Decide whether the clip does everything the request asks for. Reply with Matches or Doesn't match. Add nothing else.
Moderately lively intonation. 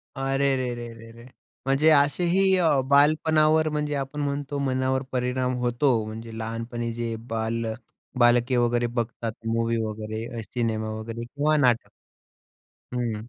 Matches